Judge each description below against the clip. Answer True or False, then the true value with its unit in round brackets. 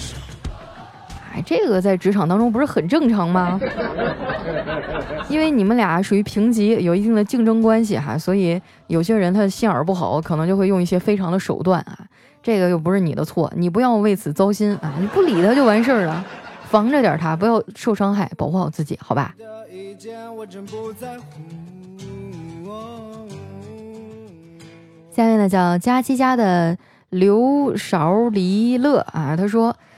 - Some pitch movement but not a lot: True (4.6 semitones)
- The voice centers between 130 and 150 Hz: False (195 Hz)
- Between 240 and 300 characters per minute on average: False (220 characters per minute)